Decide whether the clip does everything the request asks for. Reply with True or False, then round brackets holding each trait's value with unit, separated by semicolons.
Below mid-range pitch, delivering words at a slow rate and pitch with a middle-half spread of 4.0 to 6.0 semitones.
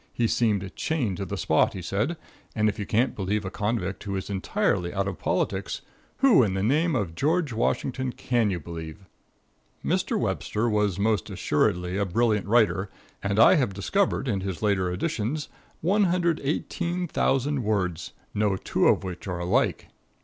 False (105 Hz; 165 wpm; 5.3 semitones)